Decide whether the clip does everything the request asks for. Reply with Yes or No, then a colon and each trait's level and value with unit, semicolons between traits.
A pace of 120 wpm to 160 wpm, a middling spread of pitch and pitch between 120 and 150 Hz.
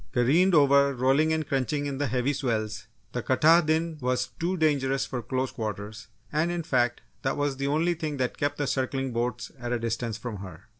No: average, 195 wpm; average, 3.7 semitones; low, 135 Hz